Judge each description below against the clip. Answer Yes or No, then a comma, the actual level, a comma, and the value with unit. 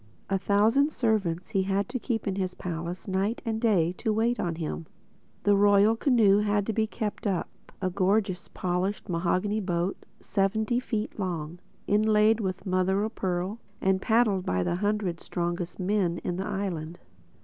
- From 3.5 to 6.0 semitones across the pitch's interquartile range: No, average, 3.1 semitones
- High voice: Yes, high, 195 Hz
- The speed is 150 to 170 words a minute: Yes, average, 160 wpm